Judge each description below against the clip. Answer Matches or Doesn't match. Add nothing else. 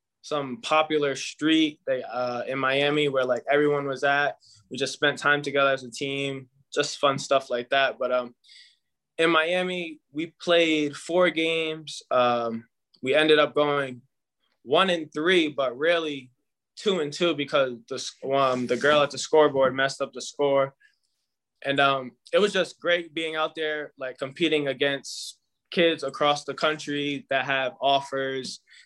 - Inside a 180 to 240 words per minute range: Doesn't match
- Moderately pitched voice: Matches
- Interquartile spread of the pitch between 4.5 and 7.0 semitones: Doesn't match